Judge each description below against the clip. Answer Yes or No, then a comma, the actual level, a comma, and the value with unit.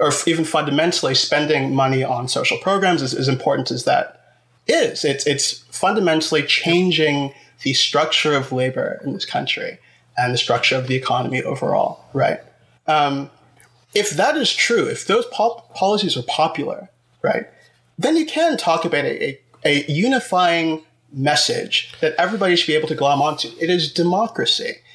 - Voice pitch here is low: No, medium, 155 Hz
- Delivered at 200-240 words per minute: No, average, 160 wpm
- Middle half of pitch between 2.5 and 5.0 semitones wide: Yes, average, 4.7 semitones